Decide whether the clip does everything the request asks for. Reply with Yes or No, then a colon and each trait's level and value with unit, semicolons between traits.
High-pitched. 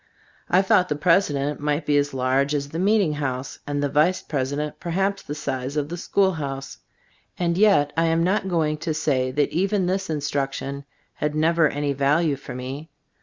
No: medium, 150 Hz